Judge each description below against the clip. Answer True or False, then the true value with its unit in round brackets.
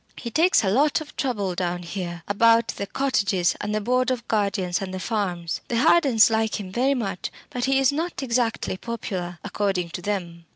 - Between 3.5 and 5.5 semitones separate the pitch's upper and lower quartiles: True (5.2 semitones)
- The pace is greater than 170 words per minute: True (195 wpm)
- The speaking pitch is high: True (210 Hz)